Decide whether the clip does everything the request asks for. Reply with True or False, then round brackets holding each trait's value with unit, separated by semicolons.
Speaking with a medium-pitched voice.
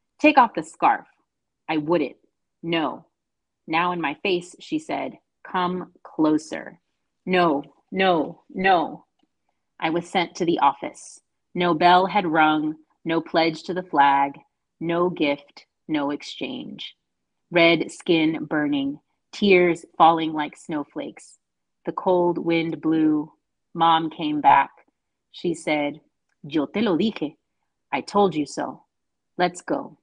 True (165 Hz)